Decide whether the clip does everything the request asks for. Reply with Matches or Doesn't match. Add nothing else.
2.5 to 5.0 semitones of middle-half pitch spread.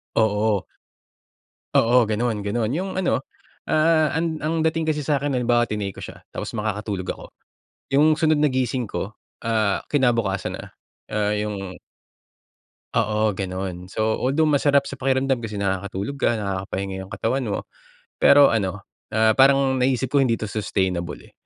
Doesn't match